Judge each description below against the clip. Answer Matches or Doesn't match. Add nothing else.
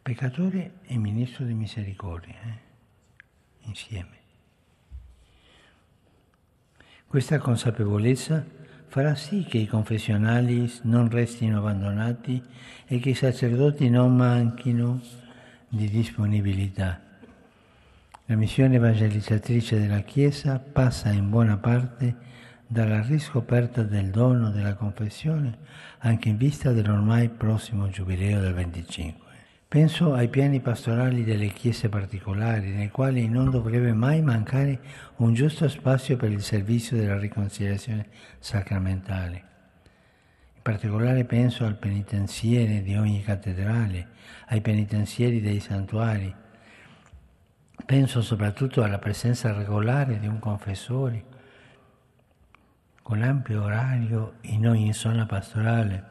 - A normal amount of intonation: Matches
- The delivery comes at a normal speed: Doesn't match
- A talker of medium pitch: Doesn't match